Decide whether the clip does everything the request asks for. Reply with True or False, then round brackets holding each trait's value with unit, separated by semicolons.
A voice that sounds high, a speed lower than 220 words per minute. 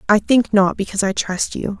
False (205 Hz; 235 wpm)